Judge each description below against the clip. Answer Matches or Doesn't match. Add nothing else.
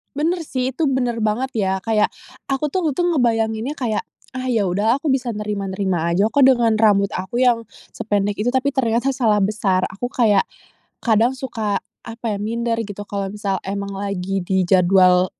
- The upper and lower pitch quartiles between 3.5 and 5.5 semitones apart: Matches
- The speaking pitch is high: Matches